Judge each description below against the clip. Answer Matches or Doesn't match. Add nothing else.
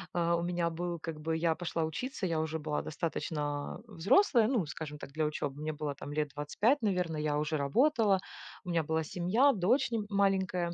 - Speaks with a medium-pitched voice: Matches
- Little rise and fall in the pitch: Doesn't match